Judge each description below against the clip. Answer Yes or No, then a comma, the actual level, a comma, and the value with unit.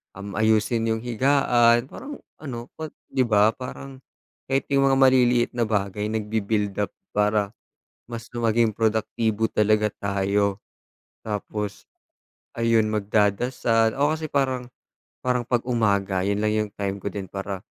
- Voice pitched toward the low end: Yes, low, 110 Hz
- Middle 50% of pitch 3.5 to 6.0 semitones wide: No, average, 2.9 semitones